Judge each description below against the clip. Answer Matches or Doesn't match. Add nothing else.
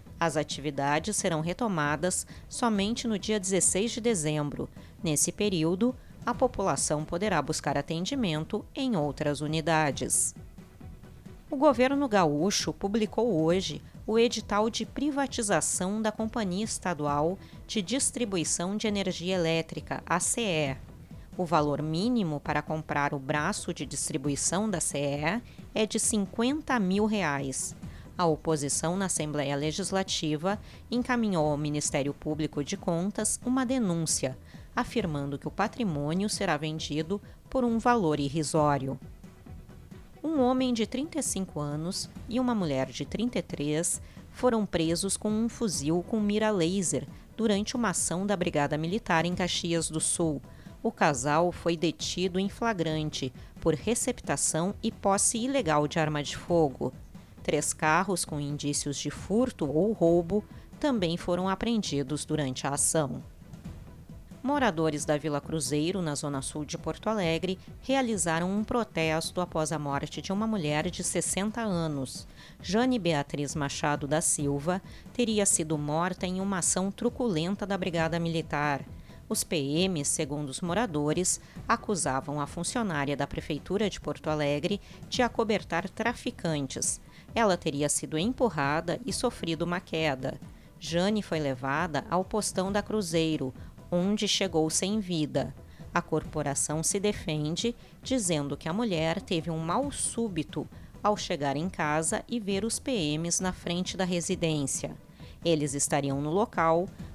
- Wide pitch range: Matches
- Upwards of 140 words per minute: Doesn't match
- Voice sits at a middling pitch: Matches